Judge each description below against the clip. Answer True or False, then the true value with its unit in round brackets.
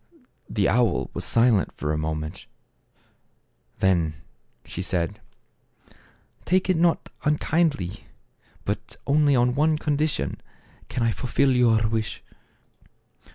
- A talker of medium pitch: False (115 Hz)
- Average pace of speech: False (110 wpm)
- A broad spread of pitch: True (7.8 semitones)